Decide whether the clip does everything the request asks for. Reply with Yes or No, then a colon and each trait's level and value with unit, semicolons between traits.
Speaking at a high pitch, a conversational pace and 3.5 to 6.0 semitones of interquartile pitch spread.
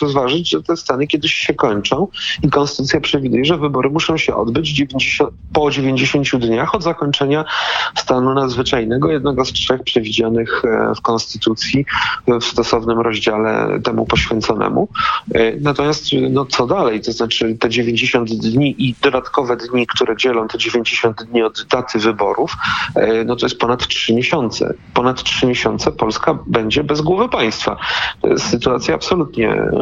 No: low, 130 Hz; average, 145 wpm; average, 3.8 semitones